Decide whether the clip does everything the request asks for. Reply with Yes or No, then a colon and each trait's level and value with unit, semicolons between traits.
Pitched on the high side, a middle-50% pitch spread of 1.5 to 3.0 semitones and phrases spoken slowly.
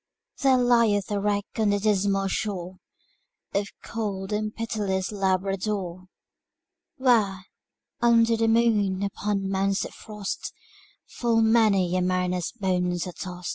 Yes: high, 200 Hz; average, 2.7 semitones; slow, 125 wpm